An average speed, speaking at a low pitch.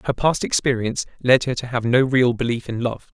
No: fast, 225 wpm; low, 125 Hz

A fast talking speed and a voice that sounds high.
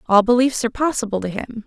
Yes: fast, 215 wpm; high, 230 Hz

